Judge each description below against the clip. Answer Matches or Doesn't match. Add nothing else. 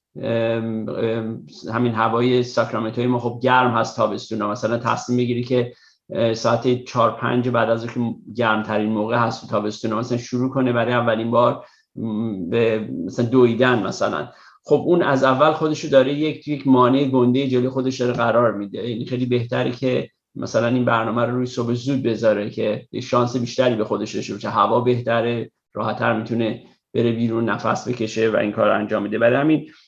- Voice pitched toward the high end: Doesn't match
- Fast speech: Matches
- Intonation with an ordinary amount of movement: Doesn't match